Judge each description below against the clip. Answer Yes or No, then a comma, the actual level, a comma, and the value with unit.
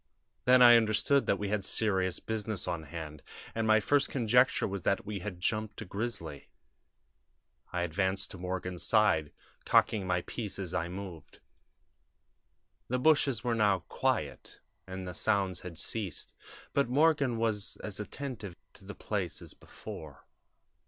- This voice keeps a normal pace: Yes, average, 150 wpm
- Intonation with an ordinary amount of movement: Yes, average, 3.9 semitones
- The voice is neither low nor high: No, low, 100 Hz